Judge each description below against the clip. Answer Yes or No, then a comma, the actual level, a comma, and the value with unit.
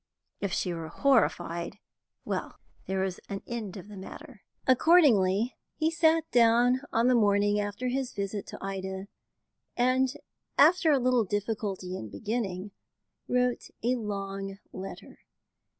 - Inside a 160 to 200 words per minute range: No, slow, 135 wpm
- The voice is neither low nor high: No, high, 210 Hz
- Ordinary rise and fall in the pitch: Yes, average, 4.4 semitones